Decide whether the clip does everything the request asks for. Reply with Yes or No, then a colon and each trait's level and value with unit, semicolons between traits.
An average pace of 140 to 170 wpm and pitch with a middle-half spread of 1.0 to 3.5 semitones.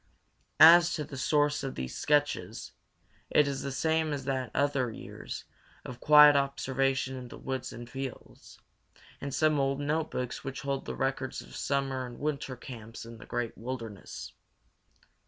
Yes: average, 165 wpm; narrow, 2.4 semitones